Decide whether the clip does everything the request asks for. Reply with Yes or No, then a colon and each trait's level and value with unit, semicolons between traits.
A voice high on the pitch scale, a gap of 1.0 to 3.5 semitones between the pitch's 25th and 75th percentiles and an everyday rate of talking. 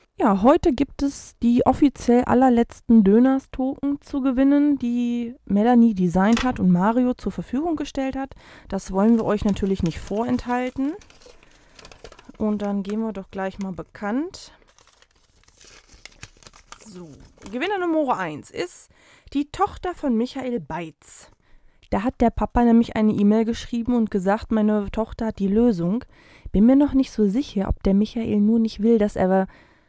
No: high, 230 Hz; average, 4.7 semitones; average, 150 wpm